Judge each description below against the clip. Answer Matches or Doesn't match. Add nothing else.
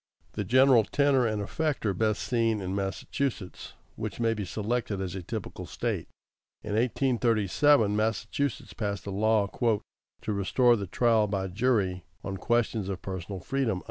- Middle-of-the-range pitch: Doesn't match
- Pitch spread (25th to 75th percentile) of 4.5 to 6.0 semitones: Doesn't match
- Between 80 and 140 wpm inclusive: Doesn't match